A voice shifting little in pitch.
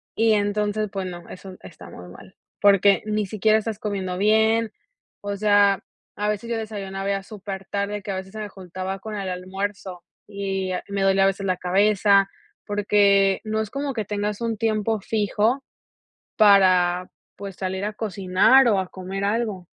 Yes: narrow, 1.8 semitones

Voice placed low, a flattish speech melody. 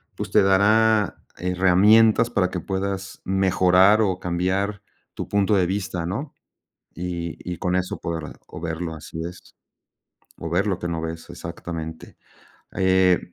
Yes: very low, 90 Hz; narrow, 2.3 semitones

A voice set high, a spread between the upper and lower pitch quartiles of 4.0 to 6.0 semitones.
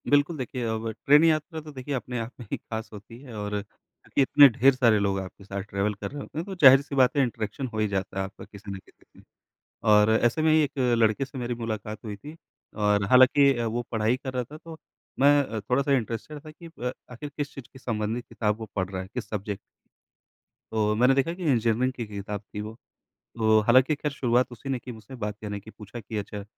No: low, 120 Hz; average, 4.4 semitones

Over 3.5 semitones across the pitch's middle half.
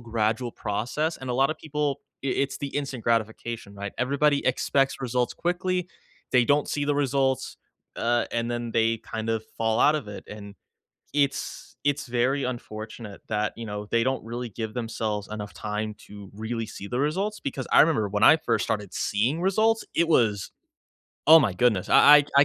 Yes: average, 4.6 semitones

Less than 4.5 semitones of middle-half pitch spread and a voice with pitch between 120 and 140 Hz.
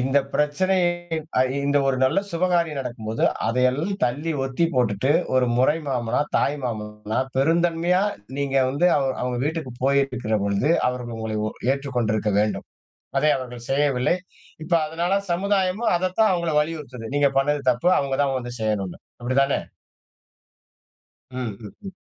No: average, 5.2 semitones; low, 135 Hz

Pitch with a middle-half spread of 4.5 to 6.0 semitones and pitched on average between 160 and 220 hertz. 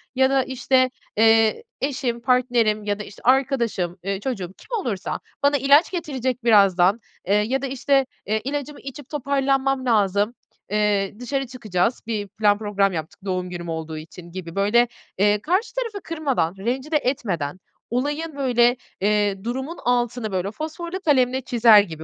No: average, 5.0 semitones; high, 240 Hz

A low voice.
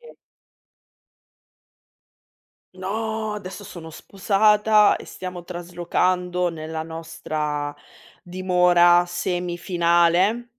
No: medium, 180 Hz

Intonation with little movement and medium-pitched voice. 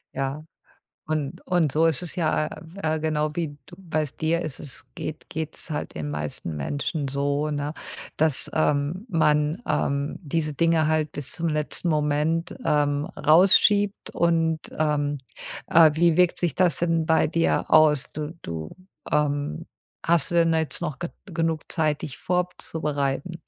Yes: narrow, 2.3 semitones; medium, 155 Hz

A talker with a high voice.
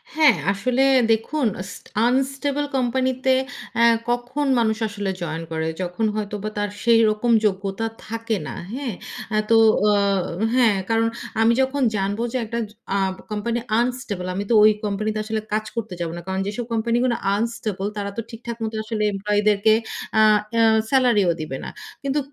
Yes: high, 225 Hz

